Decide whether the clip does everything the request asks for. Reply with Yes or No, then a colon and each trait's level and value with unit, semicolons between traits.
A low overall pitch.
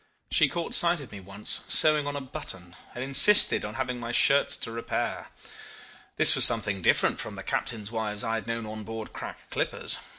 Yes: low, 115 Hz